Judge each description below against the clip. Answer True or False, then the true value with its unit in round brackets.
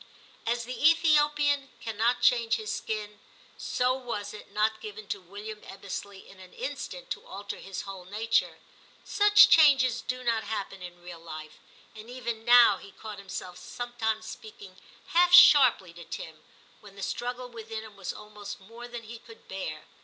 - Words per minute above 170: False (165 wpm)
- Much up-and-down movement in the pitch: False (3.7 semitones)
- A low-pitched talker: False (220 Hz)